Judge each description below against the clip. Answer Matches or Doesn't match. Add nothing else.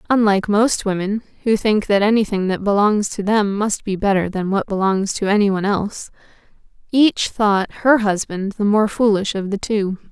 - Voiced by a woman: Matches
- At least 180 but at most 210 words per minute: Doesn't match